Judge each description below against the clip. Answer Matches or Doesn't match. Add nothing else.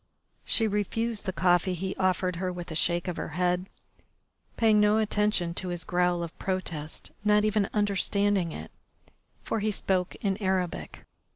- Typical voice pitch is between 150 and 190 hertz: Matches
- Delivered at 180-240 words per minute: Doesn't match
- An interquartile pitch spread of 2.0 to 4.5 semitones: Matches